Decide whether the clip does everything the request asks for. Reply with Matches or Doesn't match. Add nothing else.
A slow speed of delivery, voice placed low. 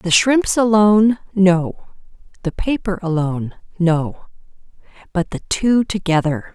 Doesn't match